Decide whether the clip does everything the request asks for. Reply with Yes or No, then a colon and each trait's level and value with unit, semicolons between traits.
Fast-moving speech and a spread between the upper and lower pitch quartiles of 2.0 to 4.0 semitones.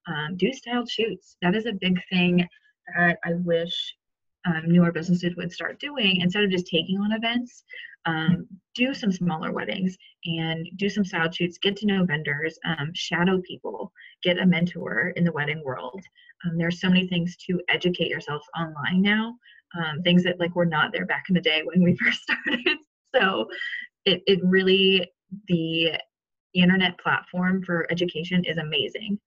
No: average, 170 wpm; narrow, 2.6 semitones